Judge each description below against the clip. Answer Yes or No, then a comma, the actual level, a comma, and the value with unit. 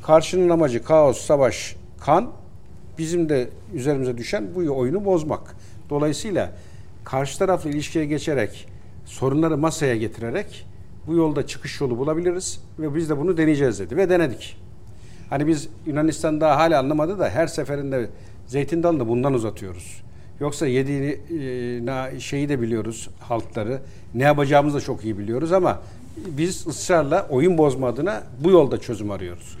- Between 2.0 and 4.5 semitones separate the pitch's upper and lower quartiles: No, wide, 5.5 semitones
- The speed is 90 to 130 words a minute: No, fast, 140 wpm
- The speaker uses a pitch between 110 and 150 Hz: Yes, medium, 140 Hz